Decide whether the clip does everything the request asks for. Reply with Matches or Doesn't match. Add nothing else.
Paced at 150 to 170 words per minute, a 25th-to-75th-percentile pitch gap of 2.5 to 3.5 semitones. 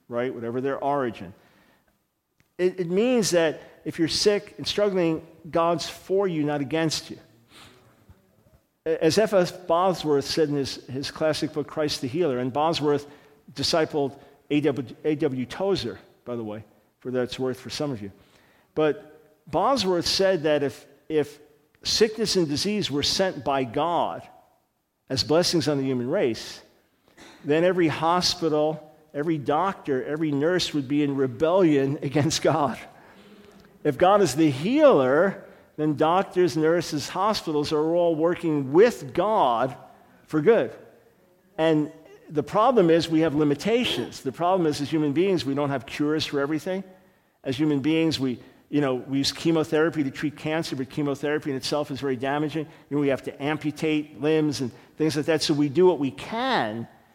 Matches